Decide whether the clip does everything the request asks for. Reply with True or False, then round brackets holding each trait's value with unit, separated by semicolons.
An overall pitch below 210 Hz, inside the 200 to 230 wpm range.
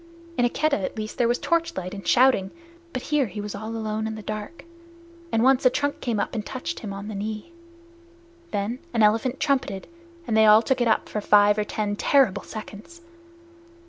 False (220 Hz; 205 wpm)